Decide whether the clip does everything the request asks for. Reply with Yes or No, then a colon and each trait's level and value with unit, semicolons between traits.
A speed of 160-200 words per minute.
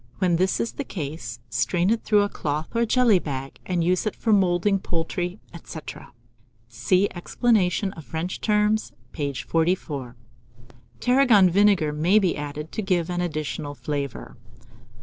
No: average, 150 wpm